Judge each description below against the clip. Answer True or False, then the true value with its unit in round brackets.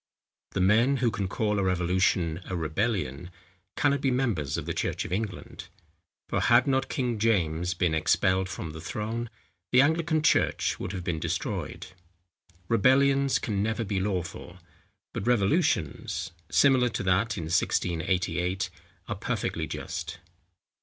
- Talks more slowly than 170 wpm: True (140 wpm)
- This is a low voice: True (100 Hz)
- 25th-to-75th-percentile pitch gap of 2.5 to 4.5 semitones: False (5.3 semitones)